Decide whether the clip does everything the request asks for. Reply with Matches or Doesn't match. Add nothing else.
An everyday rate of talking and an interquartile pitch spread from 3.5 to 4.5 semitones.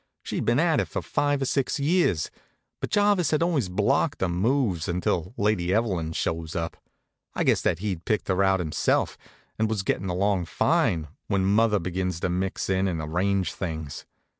Matches